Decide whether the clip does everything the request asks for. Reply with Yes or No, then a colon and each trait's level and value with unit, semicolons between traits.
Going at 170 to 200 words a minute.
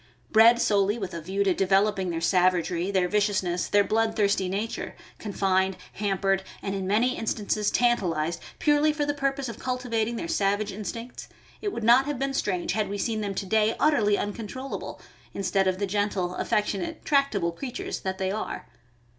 Yes: average, 175 wpm